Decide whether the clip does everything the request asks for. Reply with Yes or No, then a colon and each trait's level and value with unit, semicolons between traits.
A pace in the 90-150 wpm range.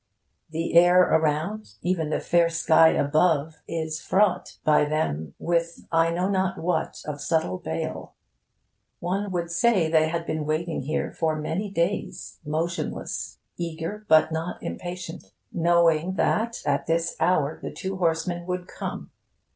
Yes: average, 140 wpm